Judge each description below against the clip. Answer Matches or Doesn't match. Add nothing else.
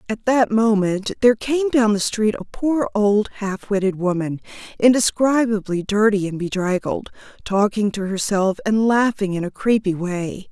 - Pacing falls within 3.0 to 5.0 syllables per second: Matches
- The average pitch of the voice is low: Doesn't match